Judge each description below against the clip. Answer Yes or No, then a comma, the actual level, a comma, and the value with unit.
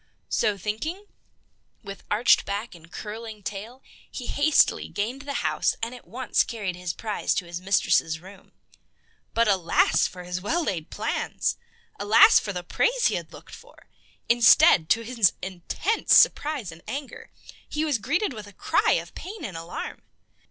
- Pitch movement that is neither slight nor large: No, wide, 5.9 semitones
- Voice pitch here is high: Yes, high, 215 Hz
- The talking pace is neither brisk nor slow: Yes, average, 160 wpm